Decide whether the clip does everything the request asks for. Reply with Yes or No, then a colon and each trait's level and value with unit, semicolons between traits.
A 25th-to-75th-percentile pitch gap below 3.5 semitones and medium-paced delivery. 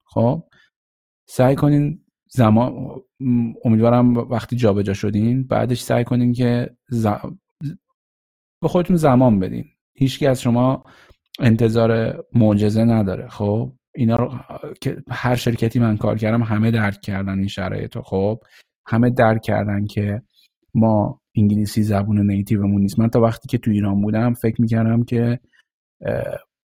Yes: average, 2.8 semitones; average, 130 wpm